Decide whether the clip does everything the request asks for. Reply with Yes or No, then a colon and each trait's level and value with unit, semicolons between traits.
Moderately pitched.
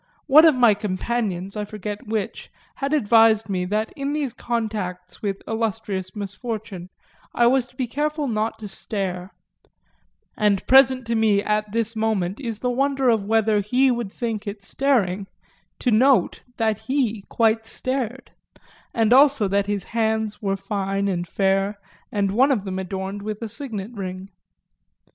No: high, 220 Hz